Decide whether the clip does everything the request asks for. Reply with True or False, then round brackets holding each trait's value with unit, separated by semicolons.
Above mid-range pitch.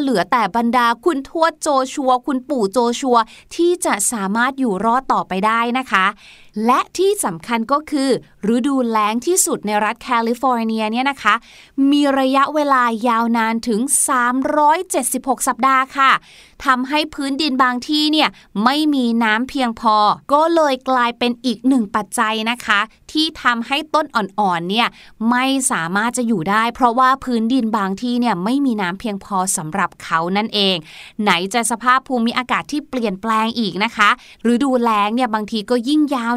True (245 Hz)